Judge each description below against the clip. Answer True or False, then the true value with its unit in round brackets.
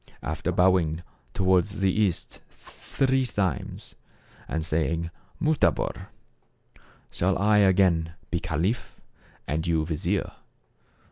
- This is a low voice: True (90 Hz)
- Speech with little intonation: False (3.5 semitones)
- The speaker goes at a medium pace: False (105 wpm)